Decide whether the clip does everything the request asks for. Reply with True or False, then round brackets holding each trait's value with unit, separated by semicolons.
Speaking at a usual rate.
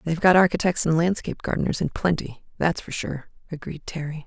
True (170 wpm)